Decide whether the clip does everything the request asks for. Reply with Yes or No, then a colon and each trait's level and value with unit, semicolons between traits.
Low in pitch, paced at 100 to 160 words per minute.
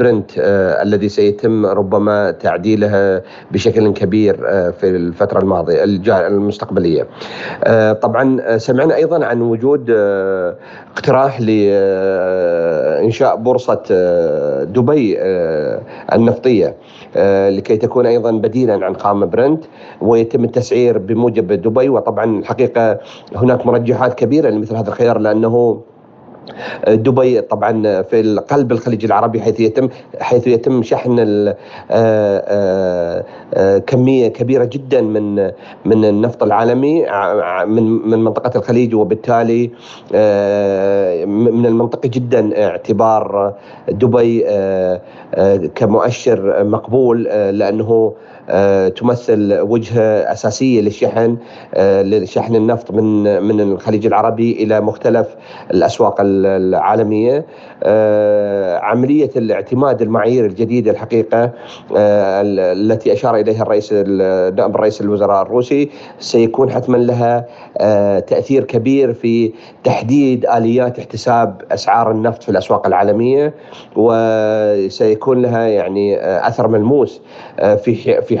Yes: low, 115 Hz; average, 105 wpm